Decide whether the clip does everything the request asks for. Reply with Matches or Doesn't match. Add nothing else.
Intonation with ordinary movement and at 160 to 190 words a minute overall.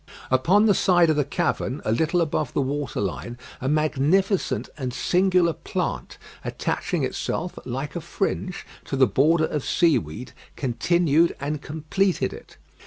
Doesn't match